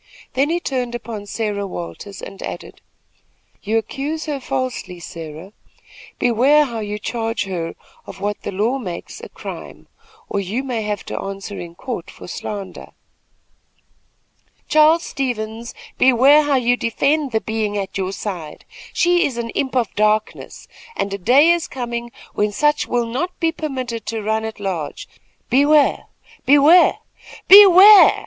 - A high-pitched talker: Yes, high, 235 Hz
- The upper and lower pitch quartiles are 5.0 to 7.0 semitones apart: Yes, average, 5.3 semitones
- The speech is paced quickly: No, average, 150 wpm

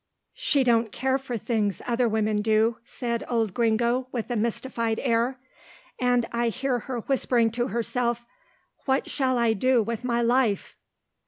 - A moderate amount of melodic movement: No, narrow, 1.8 semitones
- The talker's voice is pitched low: No, high, 235 Hz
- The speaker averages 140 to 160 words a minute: Yes, average, 155 wpm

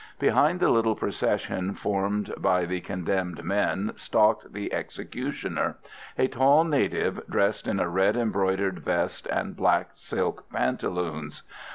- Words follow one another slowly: Yes, slow, 130 wpm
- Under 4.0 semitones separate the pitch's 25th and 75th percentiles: Yes, average, 3.2 semitones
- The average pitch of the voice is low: Yes, low, 100 Hz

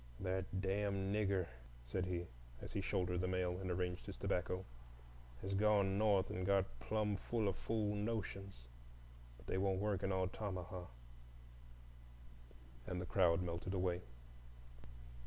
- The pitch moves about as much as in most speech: No, narrow, 1.7 semitones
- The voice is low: Yes, very low, 95 Hz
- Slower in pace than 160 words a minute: Yes, average, 140 wpm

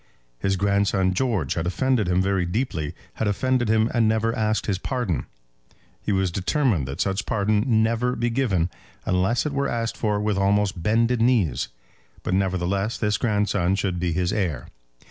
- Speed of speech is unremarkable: Yes, average, 170 wpm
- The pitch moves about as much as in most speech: Yes, average, 3.7 semitones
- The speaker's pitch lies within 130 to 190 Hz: No, low, 105 Hz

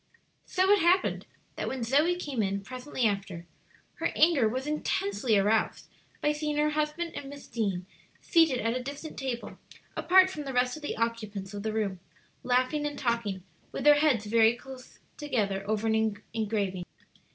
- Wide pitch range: Yes, wide, 5.7 semitones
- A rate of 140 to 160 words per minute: No, average, 170 wpm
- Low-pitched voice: No, very high, 250 Hz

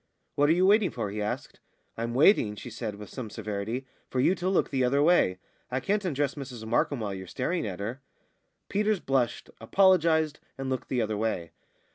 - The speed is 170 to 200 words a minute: Yes, average, 195 wpm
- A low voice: Yes, low, 130 Hz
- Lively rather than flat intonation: Yes, wide, 6.6 semitones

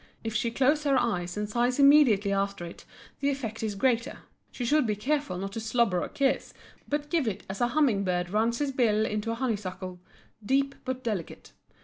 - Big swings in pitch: No, average, 5.0 semitones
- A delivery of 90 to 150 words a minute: No, average, 200 wpm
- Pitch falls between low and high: No, high, 230 Hz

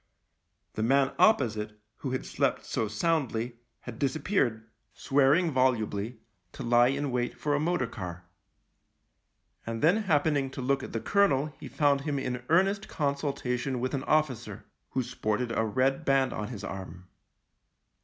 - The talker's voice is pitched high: No, low, 130 Hz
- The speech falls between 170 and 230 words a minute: No, average, 155 wpm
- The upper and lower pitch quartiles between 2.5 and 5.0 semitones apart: Yes, average, 4.0 semitones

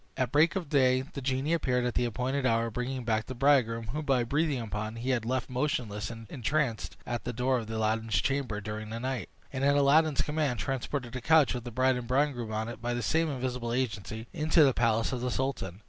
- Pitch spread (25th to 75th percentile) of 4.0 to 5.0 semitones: No, average, 3.2 semitones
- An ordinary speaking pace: No, fast, 225 wpm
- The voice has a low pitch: Yes, low, 125 Hz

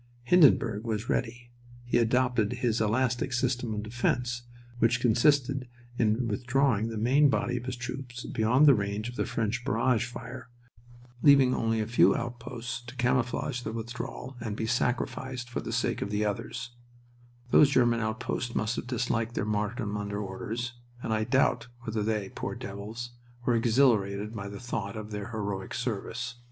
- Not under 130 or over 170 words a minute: Yes, average, 165 wpm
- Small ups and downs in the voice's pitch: Yes, narrow, 2.3 semitones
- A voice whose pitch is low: Yes, low, 120 Hz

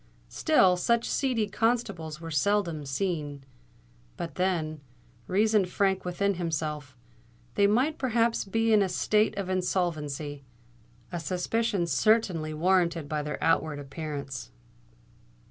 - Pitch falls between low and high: Yes, medium, 175 Hz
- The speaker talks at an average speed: No, slow, 110 wpm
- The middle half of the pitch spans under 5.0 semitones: No, average, 5.3 semitones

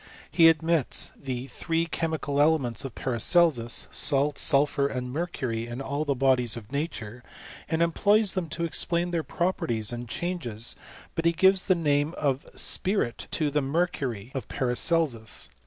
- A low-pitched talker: No, medium, 145 Hz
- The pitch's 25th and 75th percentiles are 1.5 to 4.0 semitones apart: No, average, 5.2 semitones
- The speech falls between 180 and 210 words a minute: No, average, 150 wpm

